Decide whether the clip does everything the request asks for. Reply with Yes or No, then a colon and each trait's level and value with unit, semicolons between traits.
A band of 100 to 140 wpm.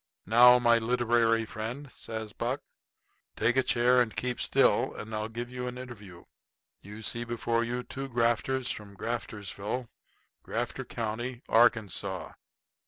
Yes: slow, 135 wpm